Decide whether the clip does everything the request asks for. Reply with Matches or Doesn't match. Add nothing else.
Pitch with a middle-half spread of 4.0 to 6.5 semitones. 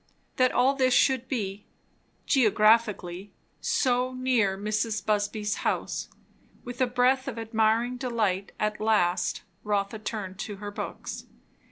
Doesn't match